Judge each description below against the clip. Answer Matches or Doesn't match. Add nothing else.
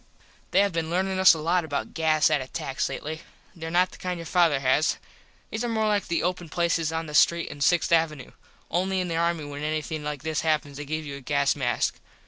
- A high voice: Doesn't match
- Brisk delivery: Matches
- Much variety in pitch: Doesn't match